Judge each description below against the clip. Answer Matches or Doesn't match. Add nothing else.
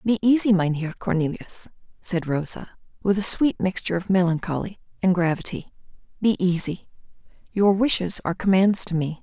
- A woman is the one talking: Matches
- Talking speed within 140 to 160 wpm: Matches